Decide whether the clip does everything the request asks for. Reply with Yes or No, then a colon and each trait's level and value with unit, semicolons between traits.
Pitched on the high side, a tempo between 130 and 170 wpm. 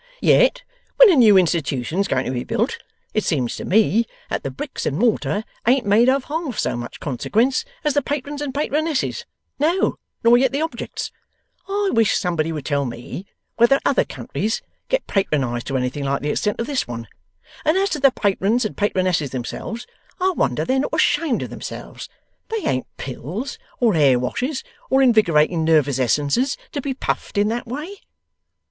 No: high, 220 Hz; average, 180 wpm